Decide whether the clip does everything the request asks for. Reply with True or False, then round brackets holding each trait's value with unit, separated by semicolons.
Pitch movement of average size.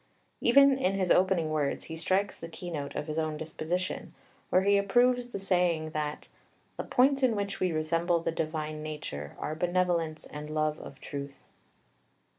True (3.9 semitones)